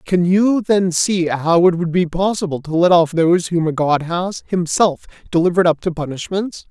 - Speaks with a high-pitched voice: No, medium, 175 Hz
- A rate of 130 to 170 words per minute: No, average, 195 wpm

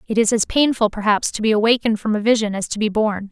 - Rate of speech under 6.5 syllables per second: No, 6.6 syllables/s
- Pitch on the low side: No, high, 215 Hz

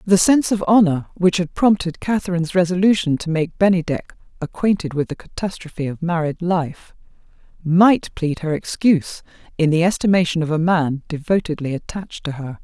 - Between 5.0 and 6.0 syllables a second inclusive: Yes, 5.5 syllables/s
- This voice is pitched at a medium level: Yes, medium, 170 Hz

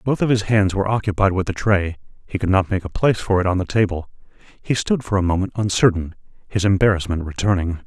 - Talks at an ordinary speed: No, fast, 220 wpm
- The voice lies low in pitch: Yes, very low, 95 Hz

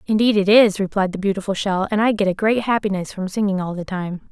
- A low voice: No, high, 200 Hz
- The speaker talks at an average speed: No, fast, 250 wpm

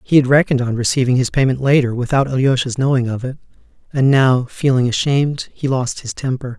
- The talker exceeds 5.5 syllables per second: Yes, 5.9 syllables/s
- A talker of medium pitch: No, low, 130 Hz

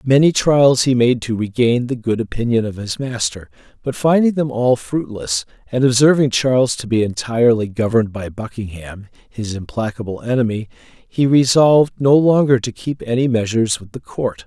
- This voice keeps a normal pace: Yes, average, 165 wpm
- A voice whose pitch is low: Yes, low, 120 Hz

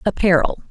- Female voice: Yes, female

